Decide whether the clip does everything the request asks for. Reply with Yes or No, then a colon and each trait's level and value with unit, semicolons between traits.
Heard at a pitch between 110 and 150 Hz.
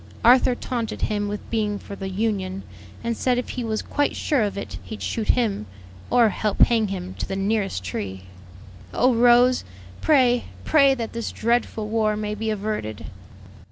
No: high, 220 Hz